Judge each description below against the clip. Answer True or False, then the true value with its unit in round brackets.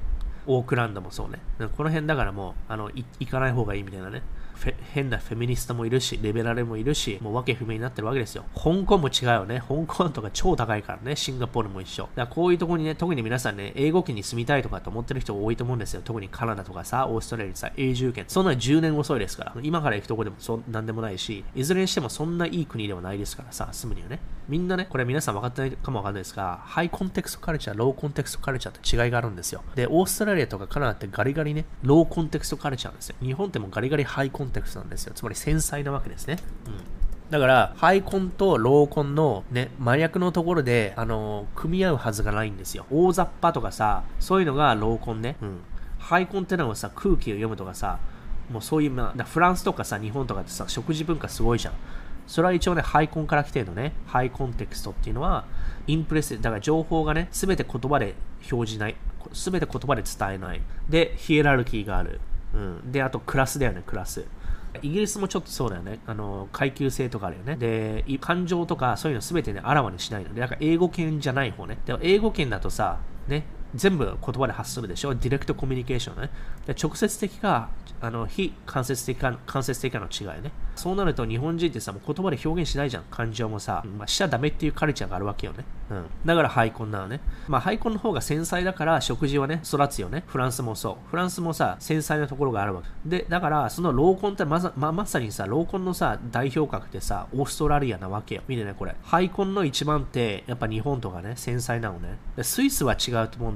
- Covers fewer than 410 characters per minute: False (485 characters per minute)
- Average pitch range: False (6.1 semitones)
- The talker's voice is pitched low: True (130 Hz)